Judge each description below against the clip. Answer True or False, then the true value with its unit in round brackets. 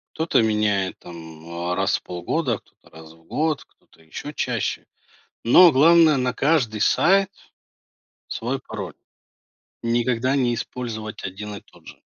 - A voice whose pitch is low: True (115 Hz)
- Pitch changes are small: False (5.6 semitones)